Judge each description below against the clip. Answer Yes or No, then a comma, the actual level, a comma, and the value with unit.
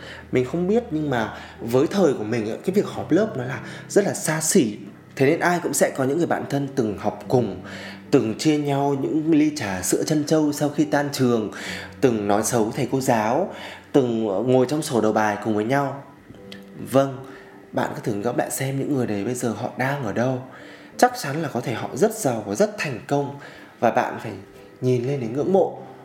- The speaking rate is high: No, average, 220 wpm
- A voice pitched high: No, low, 125 Hz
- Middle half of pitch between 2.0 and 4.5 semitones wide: No, average, 5.1 semitones